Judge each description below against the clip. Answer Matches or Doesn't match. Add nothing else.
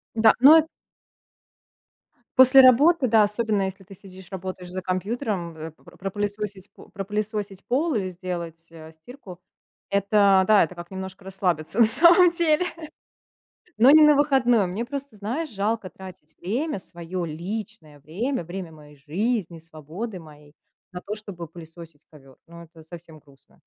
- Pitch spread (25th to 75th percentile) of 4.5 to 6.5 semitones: Matches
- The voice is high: Matches